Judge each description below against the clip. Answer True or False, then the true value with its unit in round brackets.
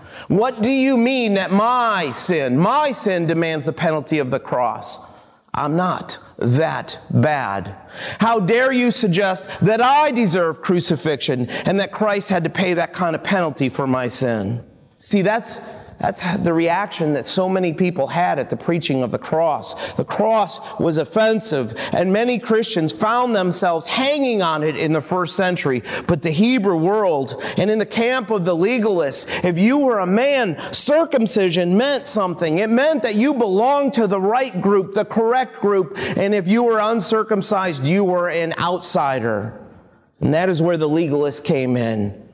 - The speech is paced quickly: False (170 wpm)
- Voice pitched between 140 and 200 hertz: True (190 Hz)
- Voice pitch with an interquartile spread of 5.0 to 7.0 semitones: True (5.3 semitones)